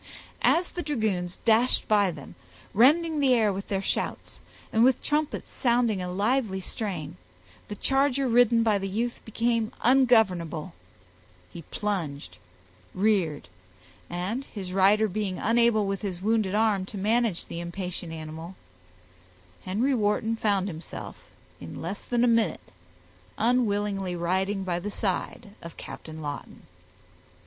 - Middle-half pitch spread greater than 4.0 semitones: Yes, average, 4.5 semitones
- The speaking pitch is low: No, high, 205 Hz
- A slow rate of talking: Yes, slow, 130 wpm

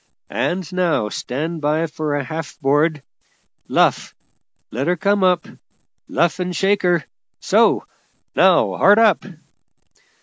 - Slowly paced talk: Yes, slow, 125 wpm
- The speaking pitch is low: No, medium, 165 Hz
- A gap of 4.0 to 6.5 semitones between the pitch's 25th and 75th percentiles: No, average, 3.6 semitones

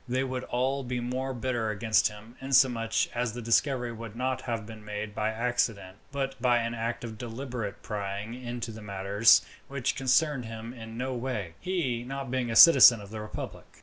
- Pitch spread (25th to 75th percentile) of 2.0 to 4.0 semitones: Yes, average, 2.7 semitones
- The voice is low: Yes, low, 120 Hz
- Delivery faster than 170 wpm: Yes, average, 185 wpm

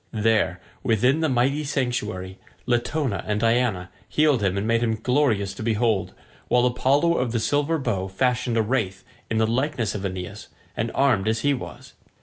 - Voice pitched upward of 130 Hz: No, low, 115 Hz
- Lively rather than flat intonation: No, average, 3.9 semitones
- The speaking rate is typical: Yes, average, 170 wpm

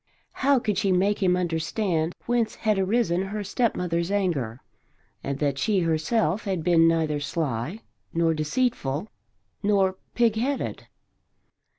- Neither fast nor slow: No, slow, 120 wpm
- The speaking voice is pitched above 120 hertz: Yes, medium, 185 Hz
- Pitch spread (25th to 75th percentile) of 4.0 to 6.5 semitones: Yes, average, 4.8 semitones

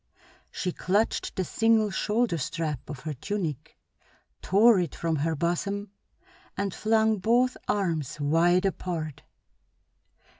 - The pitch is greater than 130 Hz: Yes, medium, 185 Hz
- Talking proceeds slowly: Yes, slow, 115 wpm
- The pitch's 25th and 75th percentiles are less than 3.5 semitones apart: No, average, 4.7 semitones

